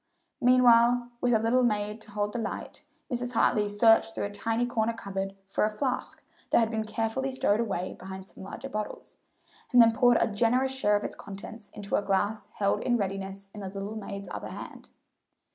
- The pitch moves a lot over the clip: No, average, 2.9 semitones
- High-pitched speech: Yes, high, 220 Hz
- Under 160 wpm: No, average, 195 wpm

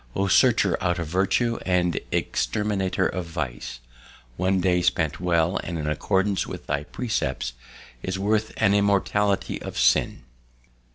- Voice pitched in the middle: No, very low, 95 Hz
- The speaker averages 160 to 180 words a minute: No, slow, 135 wpm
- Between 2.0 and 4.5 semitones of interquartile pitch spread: Yes, average, 3.0 semitones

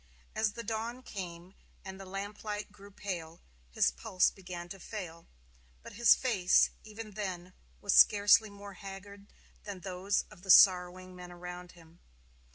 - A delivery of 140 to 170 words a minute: Yes, average, 150 wpm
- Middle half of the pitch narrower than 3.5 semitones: Yes, narrow, 2.4 semitones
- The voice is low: No, high, 195 Hz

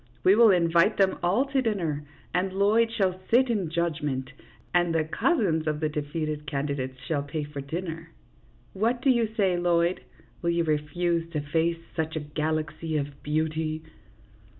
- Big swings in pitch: No, average, 3.8 semitones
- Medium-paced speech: Yes, average, 170 wpm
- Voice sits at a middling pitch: Yes, medium, 165 Hz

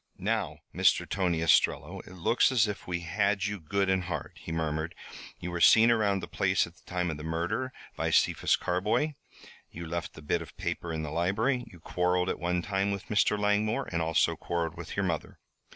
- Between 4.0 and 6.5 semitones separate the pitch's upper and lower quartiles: No, average, 3.6 semitones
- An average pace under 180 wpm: No, fast, 205 wpm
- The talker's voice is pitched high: No, very low, 90 Hz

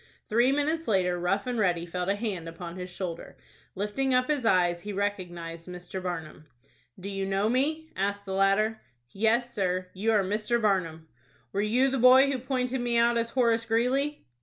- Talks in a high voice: Yes, high, 205 Hz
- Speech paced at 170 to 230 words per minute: Yes, average, 185 wpm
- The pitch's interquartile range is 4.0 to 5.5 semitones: Yes, average, 5.0 semitones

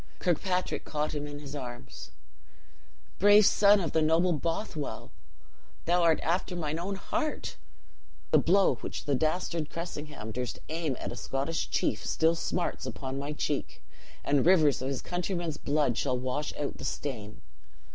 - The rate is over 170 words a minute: No, average, 155 wpm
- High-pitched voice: No, medium, 155 Hz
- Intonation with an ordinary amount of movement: Yes, average, 3.8 semitones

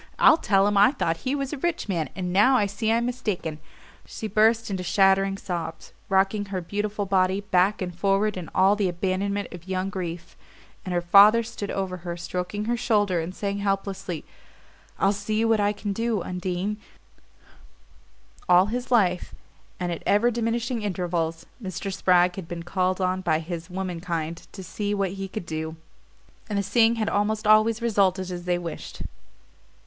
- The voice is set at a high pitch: Yes, high, 195 Hz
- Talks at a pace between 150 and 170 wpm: No, average, 180 wpm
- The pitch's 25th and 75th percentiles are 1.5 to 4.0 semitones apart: Yes, average, 2.9 semitones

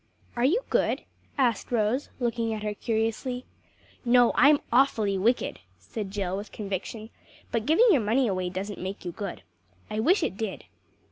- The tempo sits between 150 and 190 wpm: Yes, average, 160 wpm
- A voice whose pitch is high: Yes, high, 225 Hz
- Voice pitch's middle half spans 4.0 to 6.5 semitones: No, average, 3.6 semitones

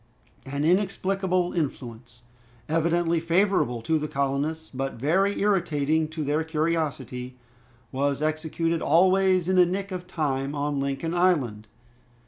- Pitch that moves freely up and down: No, average, 4.3 semitones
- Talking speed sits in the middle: No, slow, 120 wpm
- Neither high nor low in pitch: Yes, medium, 160 Hz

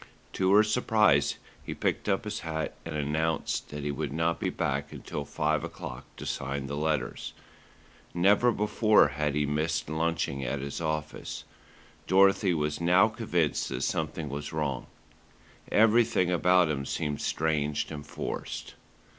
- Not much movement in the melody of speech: No, average, 4.1 semitones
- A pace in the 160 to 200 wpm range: No, average, 145 wpm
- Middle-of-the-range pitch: No, very low, 80 Hz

